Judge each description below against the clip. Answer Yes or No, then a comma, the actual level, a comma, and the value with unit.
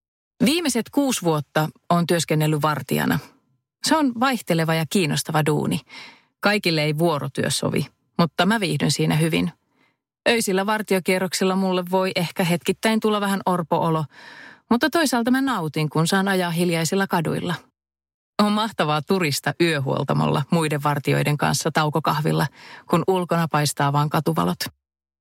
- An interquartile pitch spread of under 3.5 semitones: No, average, 4.5 semitones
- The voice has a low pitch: No, medium, 170 Hz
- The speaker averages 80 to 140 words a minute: Yes, average, 125 wpm